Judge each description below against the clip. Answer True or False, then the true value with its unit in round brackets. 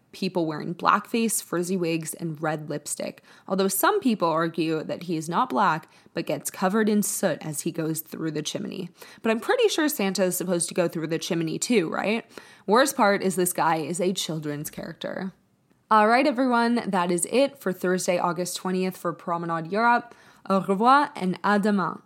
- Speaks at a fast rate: False (190 wpm)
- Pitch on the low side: False (185 Hz)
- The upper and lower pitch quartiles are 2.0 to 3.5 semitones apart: False (4.1 semitones)